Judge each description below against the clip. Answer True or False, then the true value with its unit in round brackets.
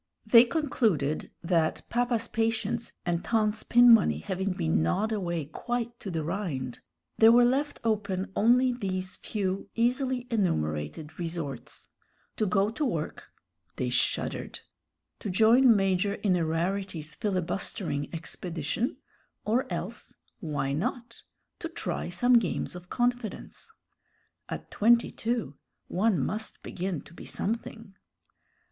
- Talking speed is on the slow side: True (120 wpm)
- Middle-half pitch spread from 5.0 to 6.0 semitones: True (5.5 semitones)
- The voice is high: True (200 Hz)